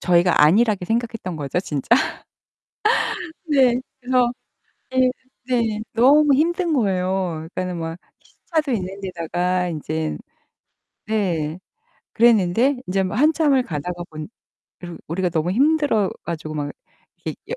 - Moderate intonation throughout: No, wide, 6.5 semitones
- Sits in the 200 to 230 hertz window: No, high, 190 Hz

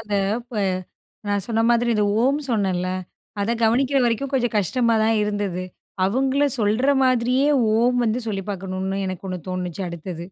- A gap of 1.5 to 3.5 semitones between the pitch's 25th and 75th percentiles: No, average, 4.2 semitones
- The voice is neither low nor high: No, high, 220 Hz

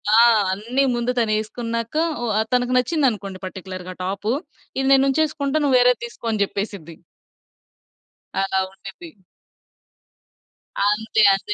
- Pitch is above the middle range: Yes, high, 225 Hz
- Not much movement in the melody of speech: No, average, 4.4 semitones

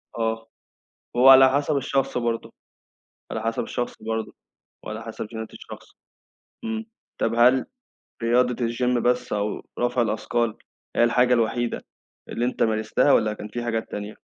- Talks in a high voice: No, low, 120 Hz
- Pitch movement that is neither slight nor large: No, narrow, 1.9 semitones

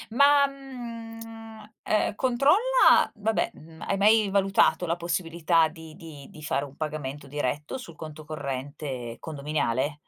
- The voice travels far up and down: Yes, wide, 7.2 semitones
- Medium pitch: Yes, medium, 165 Hz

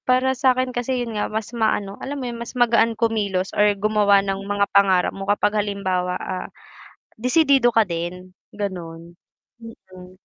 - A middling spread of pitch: Yes, average, 4.0 semitones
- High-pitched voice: Yes, high, 210 Hz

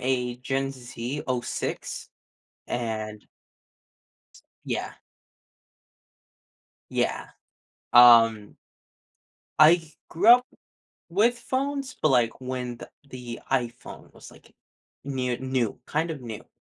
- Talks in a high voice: No, low, 125 Hz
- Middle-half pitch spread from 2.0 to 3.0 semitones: No, average, 4.3 semitones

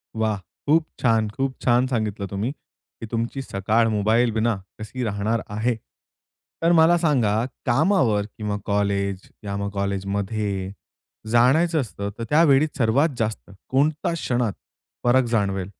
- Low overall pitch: Yes, low, 115 Hz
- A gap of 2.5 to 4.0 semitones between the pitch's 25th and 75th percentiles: No, average, 4.4 semitones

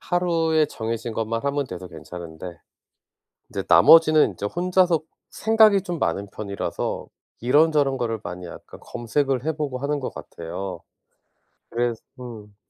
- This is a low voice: Yes, low, 125 Hz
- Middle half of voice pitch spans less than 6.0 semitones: No, wide, 7.5 semitones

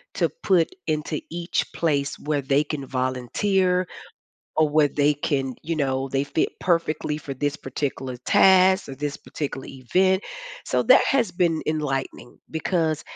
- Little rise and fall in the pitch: No, average, 3.8 semitones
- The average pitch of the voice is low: No, medium, 150 Hz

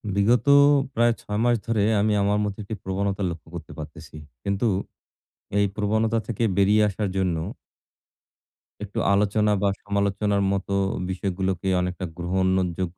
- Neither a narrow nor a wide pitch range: No, narrow, 1.9 semitones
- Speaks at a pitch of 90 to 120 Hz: Yes, low, 100 Hz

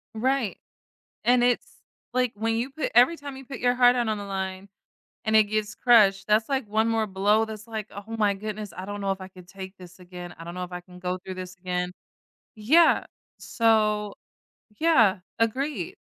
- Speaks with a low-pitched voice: No, high, 210 Hz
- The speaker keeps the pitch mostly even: No, average, 3.8 semitones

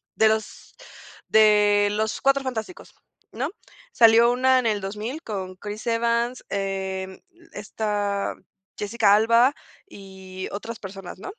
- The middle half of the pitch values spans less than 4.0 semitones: Yes, average, 2.8 semitones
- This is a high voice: Yes, high, 210 Hz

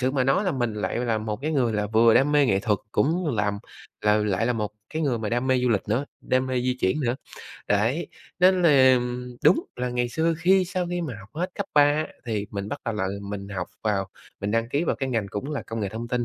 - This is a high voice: No, low, 120 Hz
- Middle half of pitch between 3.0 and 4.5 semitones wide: No, wide, 5.4 semitones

